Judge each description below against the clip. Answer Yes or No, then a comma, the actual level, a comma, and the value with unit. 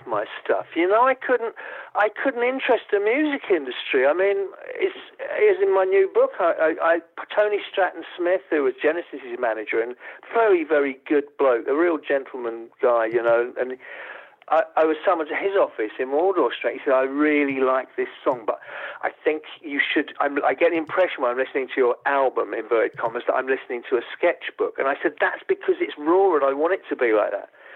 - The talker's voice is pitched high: Yes, very high, 255 Hz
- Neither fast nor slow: No, fast, 210 wpm